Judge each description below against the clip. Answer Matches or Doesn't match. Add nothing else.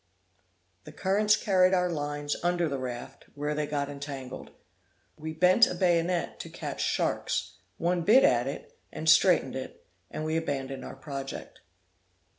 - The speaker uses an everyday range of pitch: Matches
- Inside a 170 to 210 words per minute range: Doesn't match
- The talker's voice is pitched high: Doesn't match